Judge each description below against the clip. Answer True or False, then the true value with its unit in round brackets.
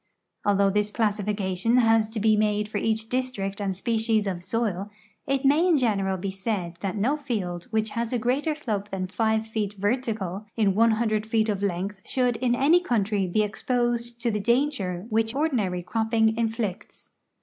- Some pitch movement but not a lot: True (3.0 semitones)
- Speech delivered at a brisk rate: False (175 wpm)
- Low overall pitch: False (220 Hz)